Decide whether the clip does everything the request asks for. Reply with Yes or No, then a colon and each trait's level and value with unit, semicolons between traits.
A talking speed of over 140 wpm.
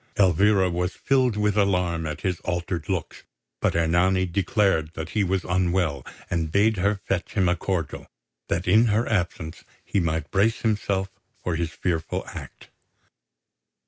Yes: average, 150 wpm